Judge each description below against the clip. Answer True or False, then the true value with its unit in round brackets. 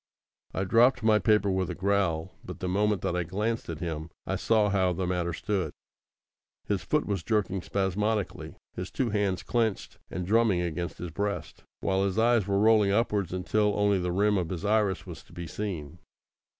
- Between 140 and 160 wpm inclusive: False (190 wpm)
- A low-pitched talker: True (100 Hz)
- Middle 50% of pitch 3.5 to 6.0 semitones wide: False (2.8 semitones)